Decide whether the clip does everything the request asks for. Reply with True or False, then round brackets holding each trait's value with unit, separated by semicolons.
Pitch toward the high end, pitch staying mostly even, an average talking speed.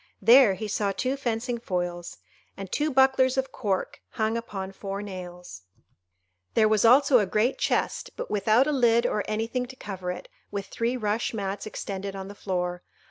False (215 Hz; 4.0 semitones; 175 wpm)